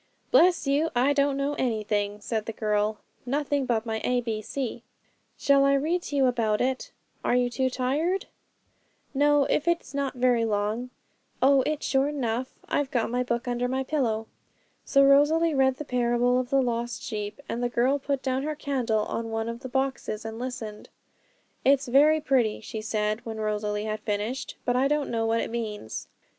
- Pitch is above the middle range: Yes, very high, 250 Hz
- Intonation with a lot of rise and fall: No, average, 3.8 semitones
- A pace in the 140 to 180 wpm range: No, average, 190 wpm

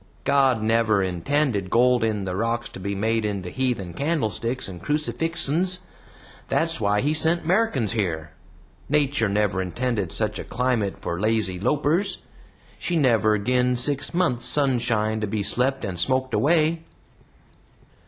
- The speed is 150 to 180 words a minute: No, average, 140 wpm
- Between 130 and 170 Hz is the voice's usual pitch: No, low, 120 Hz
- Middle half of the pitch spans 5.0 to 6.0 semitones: Yes, wide, 5.6 semitones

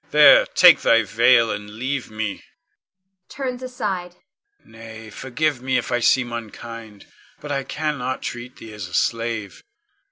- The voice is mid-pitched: No, low, 120 Hz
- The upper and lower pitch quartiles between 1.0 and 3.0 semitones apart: No, average, 4.8 semitones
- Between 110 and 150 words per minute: Yes, average, 140 wpm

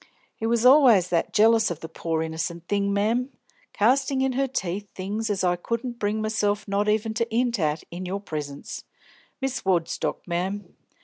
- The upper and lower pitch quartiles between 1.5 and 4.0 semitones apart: No, average, 4.7 semitones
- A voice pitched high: Yes, high, 205 Hz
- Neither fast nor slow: Yes, average, 175 wpm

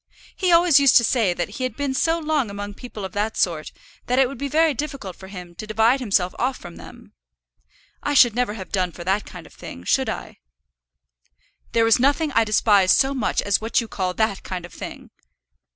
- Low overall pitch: No, high, 225 Hz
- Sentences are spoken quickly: Yes, fast, 215 wpm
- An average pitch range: No, wide, 5.9 semitones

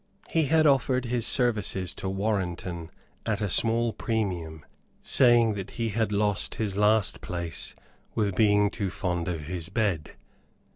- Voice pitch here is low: Yes, low, 105 Hz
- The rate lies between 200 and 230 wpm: No, average, 145 wpm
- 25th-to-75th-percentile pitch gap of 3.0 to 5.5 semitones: Yes, average, 4.0 semitones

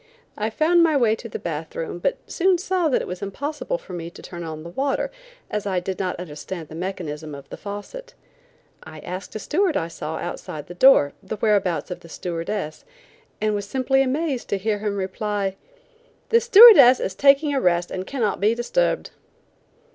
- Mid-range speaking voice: No, high, 205 Hz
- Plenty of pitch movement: Yes, wide, 7.7 semitones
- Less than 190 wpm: No, average, 195 wpm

